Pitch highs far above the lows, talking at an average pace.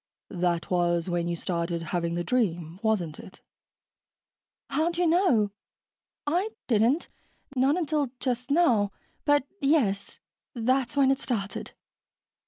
No: wide, 8.4 semitones; slow, 120 wpm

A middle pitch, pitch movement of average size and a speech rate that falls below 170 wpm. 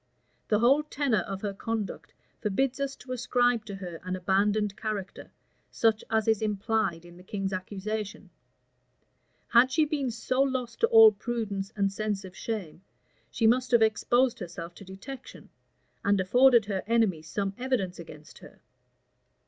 No: high, 215 Hz; average, 4.1 semitones; average, 155 wpm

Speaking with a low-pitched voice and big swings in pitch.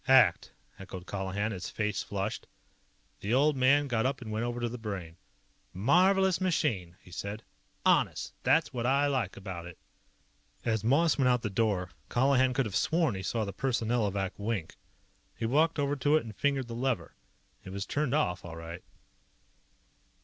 Yes: low, 115 Hz; wide, 5.7 semitones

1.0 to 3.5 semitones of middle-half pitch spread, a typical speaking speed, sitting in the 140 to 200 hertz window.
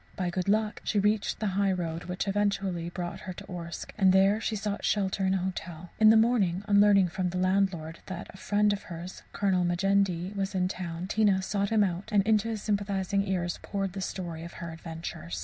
No: narrow, 2.5 semitones; fast, 220 wpm; high, 190 Hz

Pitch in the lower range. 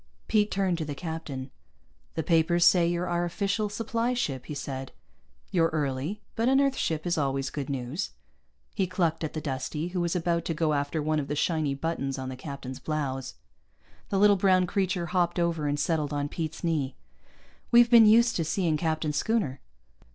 No: medium, 165 Hz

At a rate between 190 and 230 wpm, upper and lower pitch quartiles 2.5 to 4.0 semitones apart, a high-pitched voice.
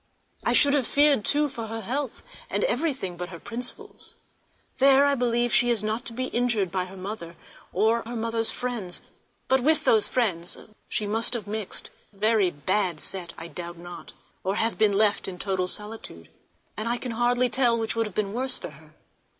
No: average, 195 wpm; average, 4.4 semitones; high, 220 Hz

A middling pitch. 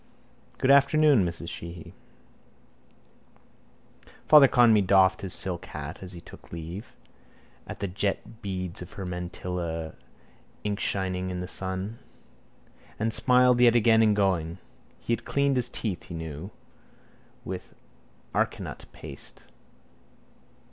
No: very low, 95 Hz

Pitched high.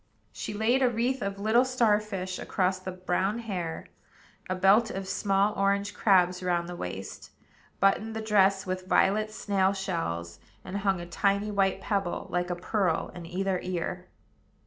Yes: high, 195 Hz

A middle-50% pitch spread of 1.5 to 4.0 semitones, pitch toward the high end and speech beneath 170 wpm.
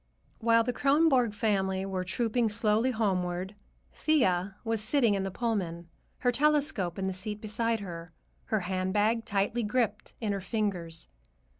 Yes: average, 3.6 semitones; high, 210 Hz; average, 145 wpm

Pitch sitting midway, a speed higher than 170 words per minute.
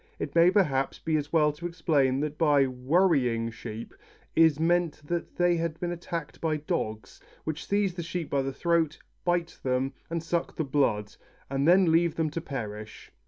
Yes: medium, 155 Hz; average, 180 wpm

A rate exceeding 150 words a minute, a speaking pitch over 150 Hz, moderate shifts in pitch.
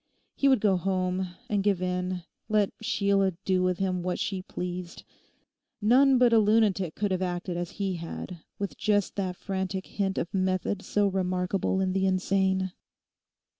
No: average, 170 wpm; high, 190 Hz; narrow, 1.7 semitones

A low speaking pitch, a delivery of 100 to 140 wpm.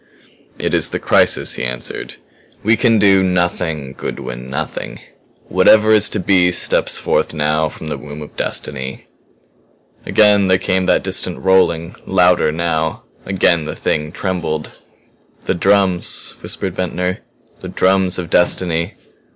Yes: very low, 90 Hz; slow, 135 wpm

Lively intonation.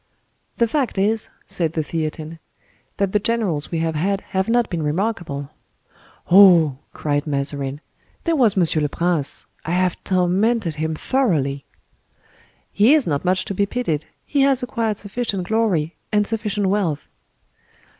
Yes: wide, 5.8 semitones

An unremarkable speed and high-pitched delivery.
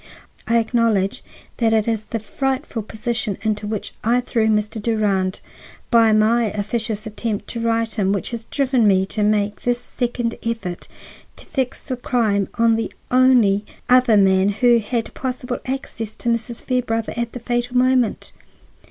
Yes: average, 160 wpm; high, 230 Hz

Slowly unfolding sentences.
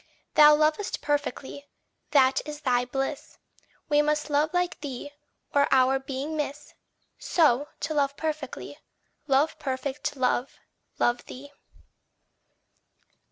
Yes: slow, 115 wpm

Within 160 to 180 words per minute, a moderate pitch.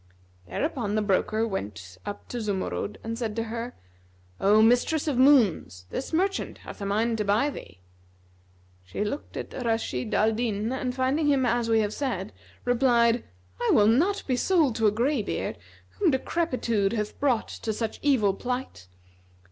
No: average, 165 wpm; high, 230 Hz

